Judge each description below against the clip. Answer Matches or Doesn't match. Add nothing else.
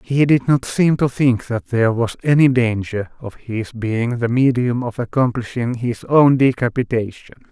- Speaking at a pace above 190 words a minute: Doesn't match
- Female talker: Doesn't match